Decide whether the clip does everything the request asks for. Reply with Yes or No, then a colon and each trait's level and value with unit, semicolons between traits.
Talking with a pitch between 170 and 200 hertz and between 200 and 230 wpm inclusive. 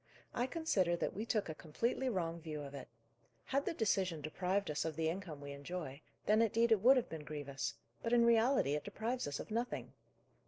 Yes: medium, 185 Hz; fast, 205 wpm